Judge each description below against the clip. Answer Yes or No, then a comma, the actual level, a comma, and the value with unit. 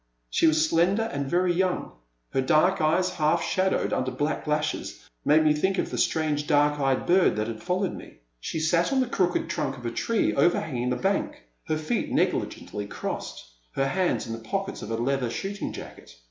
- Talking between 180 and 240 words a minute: Yes, average, 200 wpm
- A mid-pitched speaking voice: Yes, medium, 155 Hz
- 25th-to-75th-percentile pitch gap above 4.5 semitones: Yes, average, 5.3 semitones